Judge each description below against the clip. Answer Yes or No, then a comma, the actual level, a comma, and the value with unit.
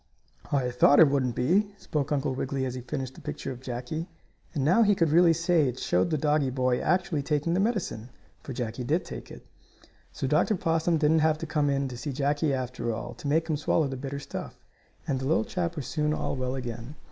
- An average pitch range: Yes, average, 3.9 semitones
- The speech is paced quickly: Yes, fast, 225 wpm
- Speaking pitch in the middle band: Yes, medium, 145 Hz